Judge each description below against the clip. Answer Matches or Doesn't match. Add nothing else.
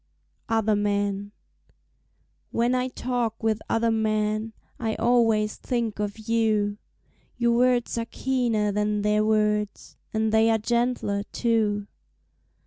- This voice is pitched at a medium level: Doesn't match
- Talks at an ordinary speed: Doesn't match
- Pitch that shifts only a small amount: Matches